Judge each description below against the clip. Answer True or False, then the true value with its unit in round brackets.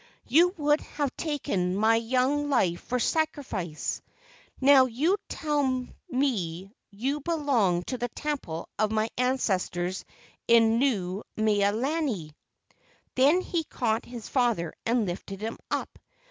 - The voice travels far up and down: True (6.0 semitones)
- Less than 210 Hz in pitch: False (240 Hz)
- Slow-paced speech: True (125 wpm)